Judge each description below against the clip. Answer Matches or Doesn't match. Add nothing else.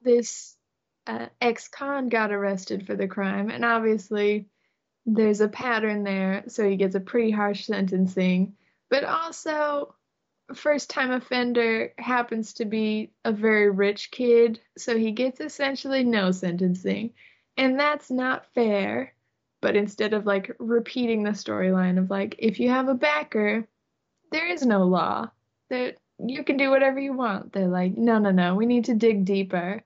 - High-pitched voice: Matches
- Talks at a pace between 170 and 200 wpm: Doesn't match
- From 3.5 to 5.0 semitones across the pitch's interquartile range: Matches